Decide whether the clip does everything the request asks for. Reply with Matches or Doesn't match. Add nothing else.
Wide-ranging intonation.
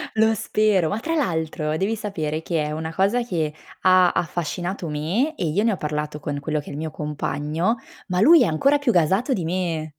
Matches